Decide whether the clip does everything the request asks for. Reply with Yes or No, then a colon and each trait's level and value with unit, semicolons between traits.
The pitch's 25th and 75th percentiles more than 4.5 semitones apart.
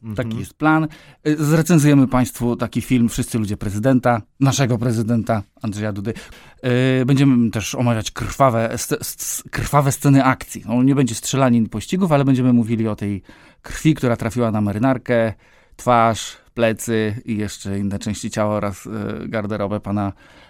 No: average, 3.5 semitones